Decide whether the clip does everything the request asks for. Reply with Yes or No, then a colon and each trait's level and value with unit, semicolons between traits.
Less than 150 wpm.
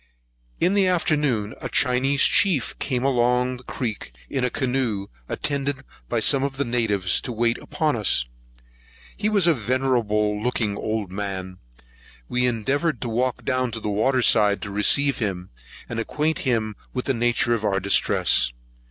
No: average, 160 wpm